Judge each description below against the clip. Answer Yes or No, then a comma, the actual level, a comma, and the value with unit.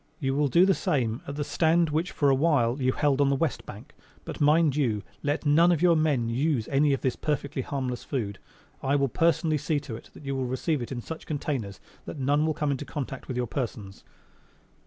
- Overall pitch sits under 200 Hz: Yes, medium, 140 Hz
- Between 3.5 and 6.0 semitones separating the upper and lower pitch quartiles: No, average, 3.1 semitones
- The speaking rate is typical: No, fast, 225 wpm